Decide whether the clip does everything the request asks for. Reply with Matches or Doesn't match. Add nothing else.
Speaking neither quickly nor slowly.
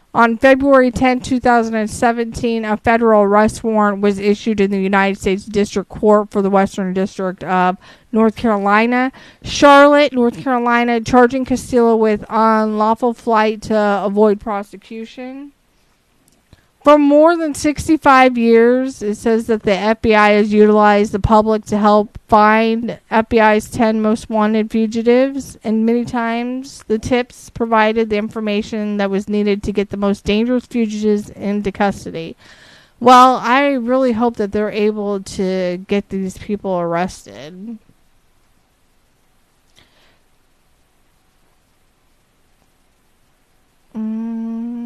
Doesn't match